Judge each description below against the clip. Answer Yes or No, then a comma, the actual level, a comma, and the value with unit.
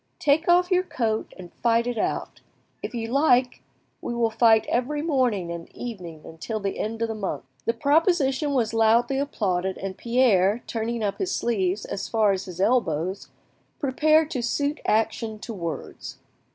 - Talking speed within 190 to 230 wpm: No, average, 165 wpm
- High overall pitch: Yes, high, 230 Hz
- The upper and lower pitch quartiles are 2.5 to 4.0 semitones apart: No, average, 4.8 semitones